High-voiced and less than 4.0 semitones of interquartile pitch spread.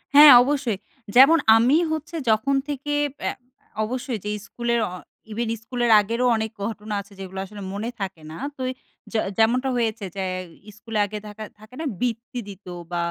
Yes: high, 225 Hz; average, 3.3 semitones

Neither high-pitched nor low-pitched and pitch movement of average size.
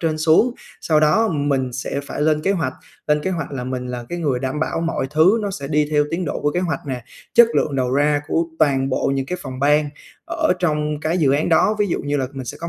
Yes: medium, 150 Hz; average, 3.3 semitones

